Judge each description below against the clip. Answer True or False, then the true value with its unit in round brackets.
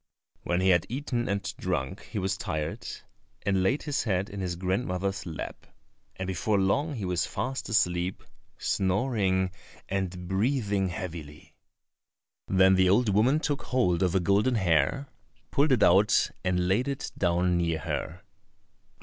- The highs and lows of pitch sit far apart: False (3.6 semitones)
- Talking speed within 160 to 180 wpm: False (150 wpm)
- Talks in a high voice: False (95 Hz)